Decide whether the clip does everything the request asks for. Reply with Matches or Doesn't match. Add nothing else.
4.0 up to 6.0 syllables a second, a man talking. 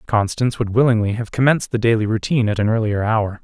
Doesn't match